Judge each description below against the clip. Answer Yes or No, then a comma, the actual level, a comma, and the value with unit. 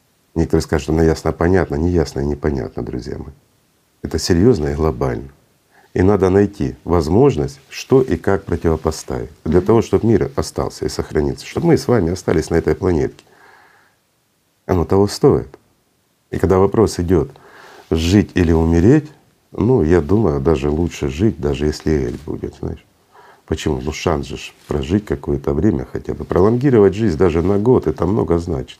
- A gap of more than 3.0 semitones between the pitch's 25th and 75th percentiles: Yes, average, 4.0 semitones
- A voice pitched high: No, very low, 85 Hz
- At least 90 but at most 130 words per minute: No, fast, 160 wpm